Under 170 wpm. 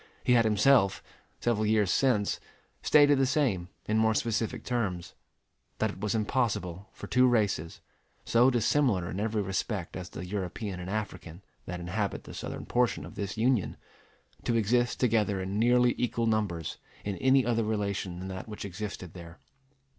Yes: average, 160 wpm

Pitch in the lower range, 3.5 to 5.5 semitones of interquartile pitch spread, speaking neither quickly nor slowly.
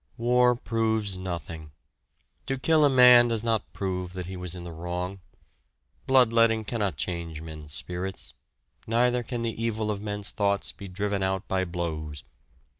Yes: low, 100 Hz; average, 4.5 semitones; average, 155 wpm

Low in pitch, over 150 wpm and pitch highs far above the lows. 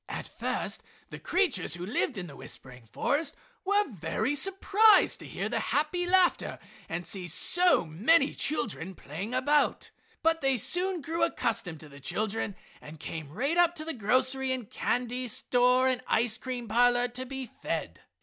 No: very high, 250 Hz; average, 165 wpm; wide, 7.9 semitones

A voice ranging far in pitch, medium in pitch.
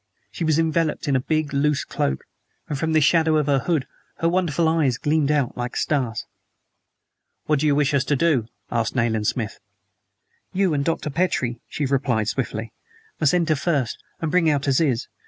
No: average, 3.6 semitones; medium, 145 Hz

